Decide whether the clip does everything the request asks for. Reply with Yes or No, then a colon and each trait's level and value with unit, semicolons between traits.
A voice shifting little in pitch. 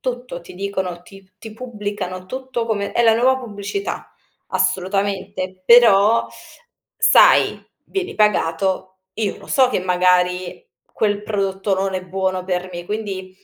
No: average, 3.1 semitones